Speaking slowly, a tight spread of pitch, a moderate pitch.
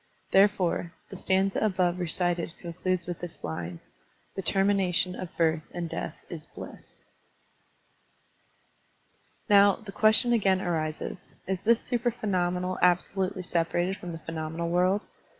Yes: slow, 130 wpm; narrow, 2.3 semitones; medium, 180 Hz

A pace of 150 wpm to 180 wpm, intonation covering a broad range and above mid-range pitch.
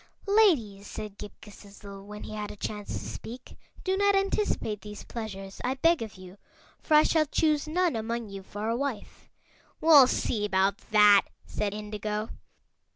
Yes: average, 165 wpm; wide, 6.1 semitones; high, 215 Hz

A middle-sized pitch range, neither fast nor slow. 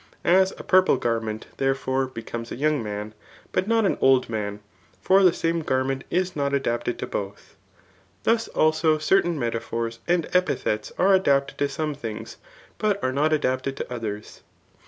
No: wide, 6.6 semitones; average, 155 wpm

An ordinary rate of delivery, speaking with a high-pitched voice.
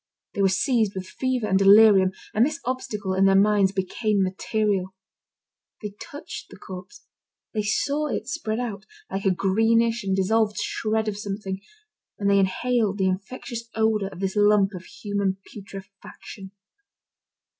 Yes: average, 150 wpm; high, 205 Hz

